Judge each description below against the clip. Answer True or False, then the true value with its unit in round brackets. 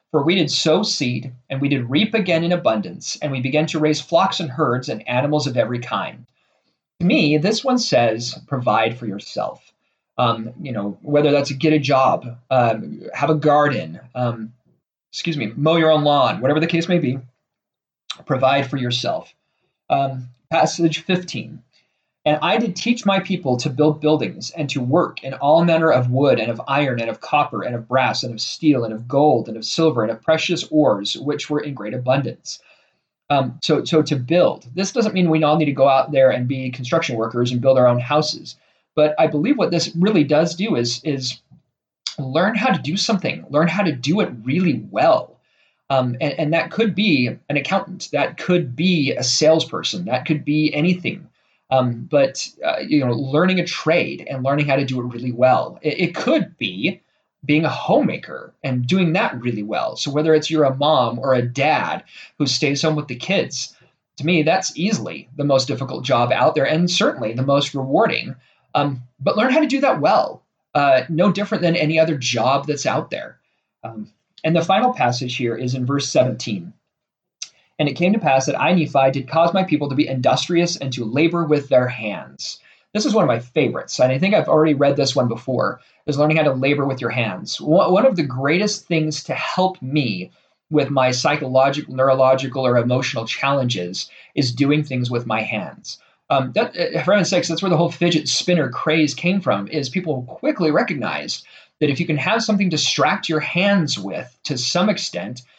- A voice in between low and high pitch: True (150 Hz)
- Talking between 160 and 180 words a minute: False (200 wpm)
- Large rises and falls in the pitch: False (4.3 semitones)